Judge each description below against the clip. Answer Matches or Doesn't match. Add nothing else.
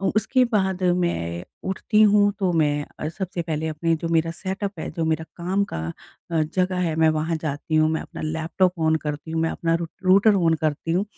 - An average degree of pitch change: Matches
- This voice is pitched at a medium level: Matches